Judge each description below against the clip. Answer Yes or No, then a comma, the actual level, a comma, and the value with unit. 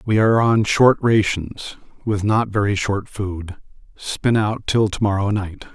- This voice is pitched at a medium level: No, low, 105 Hz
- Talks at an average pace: Yes, average, 165 wpm